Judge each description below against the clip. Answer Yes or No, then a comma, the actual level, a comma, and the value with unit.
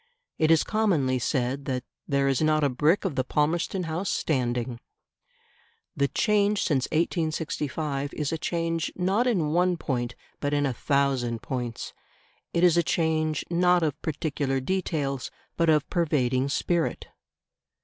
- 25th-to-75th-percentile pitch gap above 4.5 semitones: No, average, 3.8 semitones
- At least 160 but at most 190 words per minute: No, average, 145 wpm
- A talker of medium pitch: Yes, medium, 155 Hz